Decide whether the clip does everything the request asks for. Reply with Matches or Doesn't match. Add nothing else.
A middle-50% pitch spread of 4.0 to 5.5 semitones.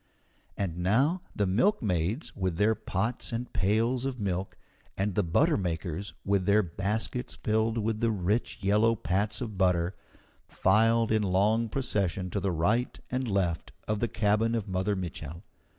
Doesn't match